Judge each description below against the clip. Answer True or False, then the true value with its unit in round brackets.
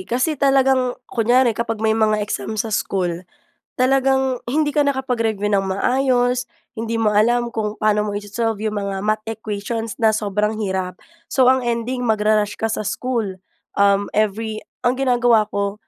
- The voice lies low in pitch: False (225 Hz)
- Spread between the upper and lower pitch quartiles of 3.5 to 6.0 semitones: False (2.9 semitones)